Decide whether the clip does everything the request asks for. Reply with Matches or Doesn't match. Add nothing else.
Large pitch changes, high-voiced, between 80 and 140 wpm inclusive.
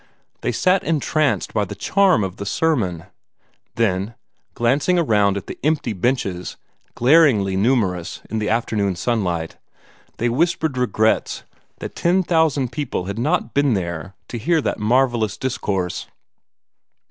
Doesn't match